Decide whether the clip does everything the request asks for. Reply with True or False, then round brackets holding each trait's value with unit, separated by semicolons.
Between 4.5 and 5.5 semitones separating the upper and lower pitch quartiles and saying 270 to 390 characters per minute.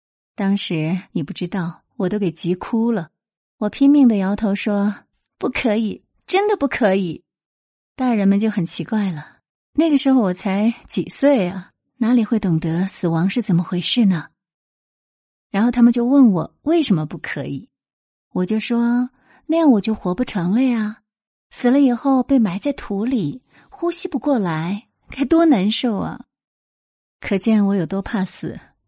False (5.2 semitones; 225 characters per minute)